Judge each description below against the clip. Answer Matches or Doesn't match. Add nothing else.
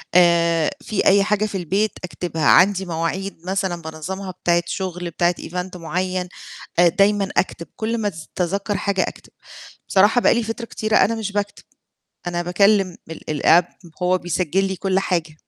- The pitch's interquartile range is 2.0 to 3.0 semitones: Matches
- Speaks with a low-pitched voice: Doesn't match